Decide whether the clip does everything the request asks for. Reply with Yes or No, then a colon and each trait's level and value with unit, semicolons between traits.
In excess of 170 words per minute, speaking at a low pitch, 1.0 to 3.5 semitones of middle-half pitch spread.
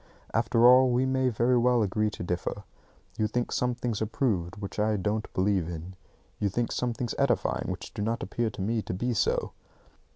Yes: average, 200 wpm; low, 110 Hz; average, 3.2 semitones